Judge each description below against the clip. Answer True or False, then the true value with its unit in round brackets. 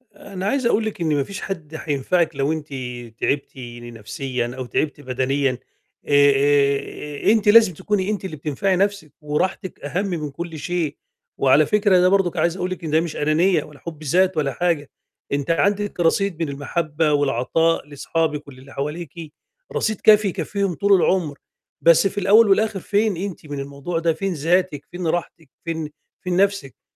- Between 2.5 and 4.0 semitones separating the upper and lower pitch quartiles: False (4.6 semitones)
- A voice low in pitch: False (165 Hz)